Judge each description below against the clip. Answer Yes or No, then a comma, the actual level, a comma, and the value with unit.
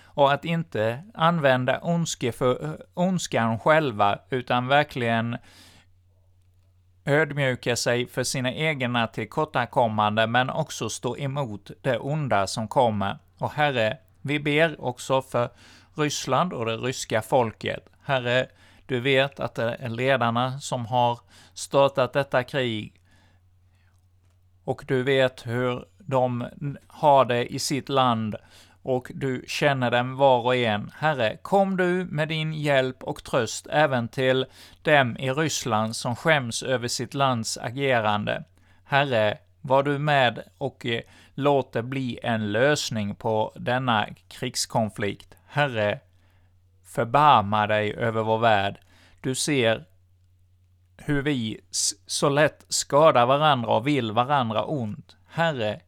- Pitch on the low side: Yes, low, 125 Hz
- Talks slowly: Yes, slow, 120 wpm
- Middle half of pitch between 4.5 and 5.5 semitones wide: Yes, average, 4.8 semitones